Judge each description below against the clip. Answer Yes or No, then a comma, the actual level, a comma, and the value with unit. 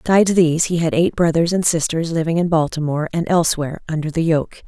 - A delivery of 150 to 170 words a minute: No, fast, 205 wpm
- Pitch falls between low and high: Yes, medium, 165 Hz